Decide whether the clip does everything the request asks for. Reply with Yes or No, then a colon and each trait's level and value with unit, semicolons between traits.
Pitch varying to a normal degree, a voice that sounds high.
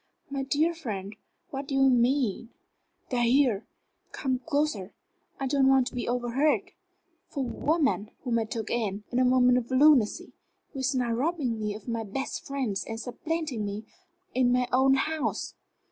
Yes: average, 3.2 semitones; very high, 255 Hz